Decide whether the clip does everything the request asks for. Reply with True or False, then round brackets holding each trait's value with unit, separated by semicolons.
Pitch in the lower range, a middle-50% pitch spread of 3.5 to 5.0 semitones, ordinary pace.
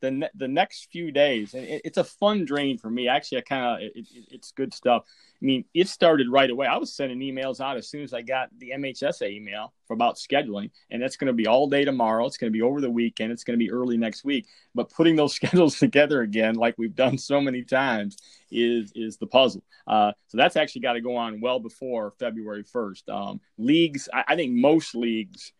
False (130 Hz; 4.1 semitones; 235 wpm)